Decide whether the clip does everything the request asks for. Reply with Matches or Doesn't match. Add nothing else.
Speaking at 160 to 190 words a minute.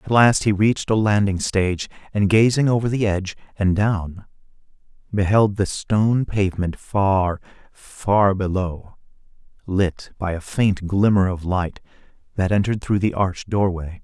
Doesn't match